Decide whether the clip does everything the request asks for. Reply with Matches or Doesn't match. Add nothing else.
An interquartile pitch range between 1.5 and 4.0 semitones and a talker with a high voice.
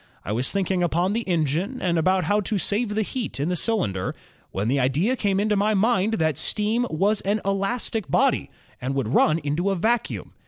Doesn't match